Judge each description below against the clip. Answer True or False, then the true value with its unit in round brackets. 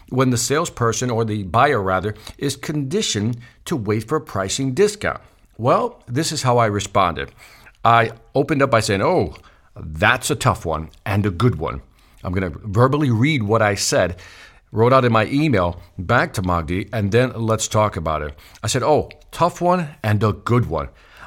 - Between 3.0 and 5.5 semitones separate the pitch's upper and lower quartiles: True (4.5 semitones)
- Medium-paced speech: True (185 wpm)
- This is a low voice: True (115 Hz)